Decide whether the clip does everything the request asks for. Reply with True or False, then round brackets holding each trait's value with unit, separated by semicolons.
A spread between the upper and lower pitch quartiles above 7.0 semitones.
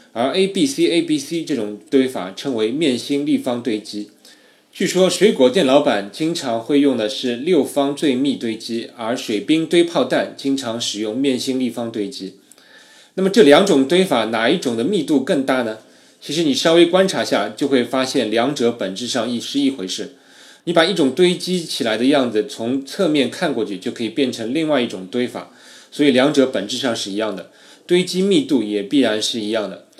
False (6.5 semitones)